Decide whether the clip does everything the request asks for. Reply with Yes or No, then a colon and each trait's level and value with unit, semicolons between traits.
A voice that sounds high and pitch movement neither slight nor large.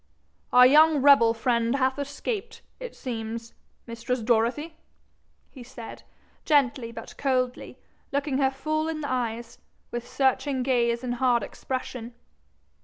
Yes: very high, 255 Hz; average, 3.1 semitones